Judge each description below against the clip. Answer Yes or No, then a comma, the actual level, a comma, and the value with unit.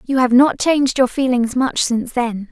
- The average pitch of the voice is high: Yes, very high, 250 Hz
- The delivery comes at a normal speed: No, fast, 215 wpm